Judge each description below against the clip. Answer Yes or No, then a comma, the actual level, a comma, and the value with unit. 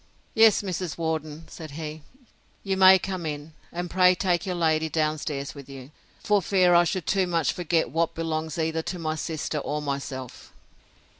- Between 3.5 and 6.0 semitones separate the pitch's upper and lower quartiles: No, average, 2.8 semitones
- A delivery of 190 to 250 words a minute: No, average, 175 wpm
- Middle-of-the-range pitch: Yes, medium, 160 Hz